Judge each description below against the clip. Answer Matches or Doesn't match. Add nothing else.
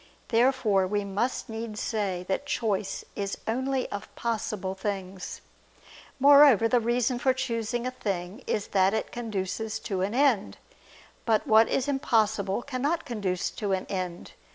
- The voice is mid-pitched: Doesn't match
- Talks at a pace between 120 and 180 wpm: Matches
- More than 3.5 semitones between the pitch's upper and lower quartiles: Matches